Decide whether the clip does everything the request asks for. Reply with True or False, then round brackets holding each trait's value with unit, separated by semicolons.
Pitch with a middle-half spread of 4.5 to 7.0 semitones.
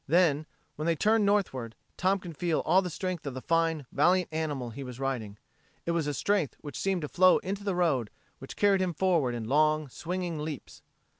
True (4.8 semitones)